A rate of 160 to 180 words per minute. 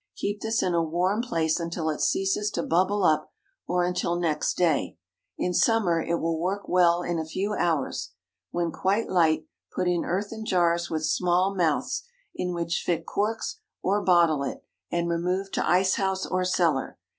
Yes: average, 175 wpm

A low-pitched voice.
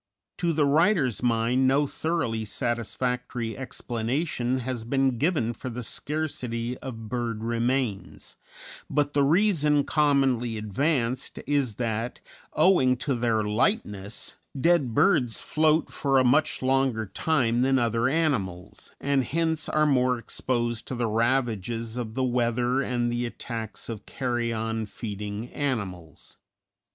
Yes: low, 125 Hz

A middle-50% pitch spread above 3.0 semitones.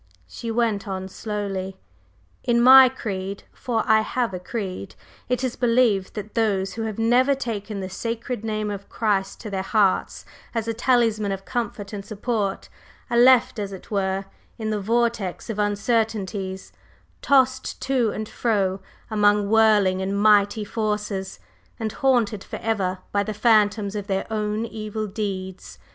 No: narrow, 2.6 semitones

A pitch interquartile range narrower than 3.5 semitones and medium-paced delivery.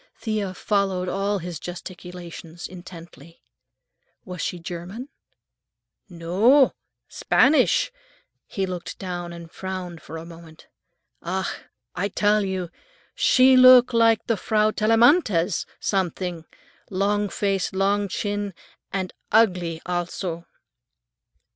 No: average, 3.1 semitones; slow, 110 wpm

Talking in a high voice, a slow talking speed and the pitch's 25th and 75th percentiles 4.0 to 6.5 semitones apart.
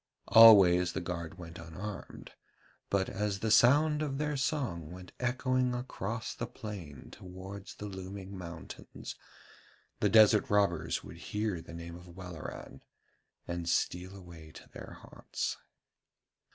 No: very low, 95 Hz; slow, 130 wpm; average, 4.5 semitones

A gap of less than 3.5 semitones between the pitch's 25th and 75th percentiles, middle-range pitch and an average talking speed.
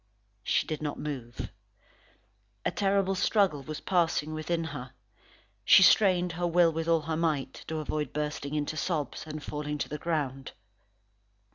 Yes: narrow, 2.6 semitones; medium, 155 Hz; average, 150 wpm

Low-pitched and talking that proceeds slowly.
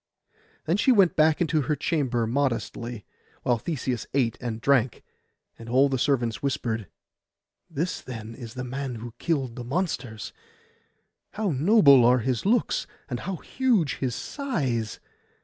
No: low, 130 Hz; average, 145 wpm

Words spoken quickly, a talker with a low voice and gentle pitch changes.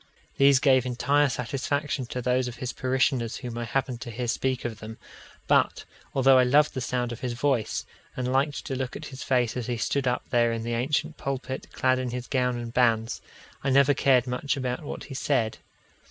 Yes: fast, 210 wpm; low, 125 Hz; narrow, 2.0 semitones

